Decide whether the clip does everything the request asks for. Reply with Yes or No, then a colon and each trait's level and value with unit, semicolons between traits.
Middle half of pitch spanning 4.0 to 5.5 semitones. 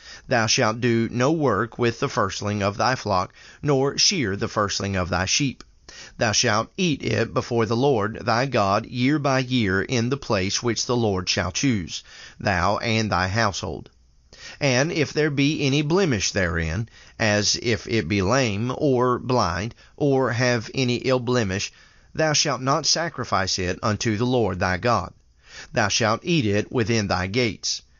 Yes: average, 4.3 semitones